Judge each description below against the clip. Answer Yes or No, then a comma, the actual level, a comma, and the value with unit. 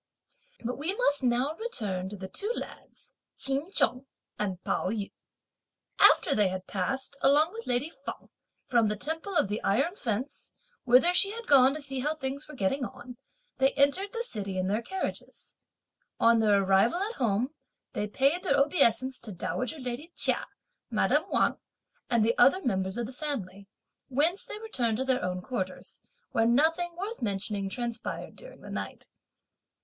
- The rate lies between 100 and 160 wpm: No, average, 170 wpm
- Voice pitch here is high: Yes, very high, 255 Hz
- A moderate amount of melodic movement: No, wide, 6.5 semitones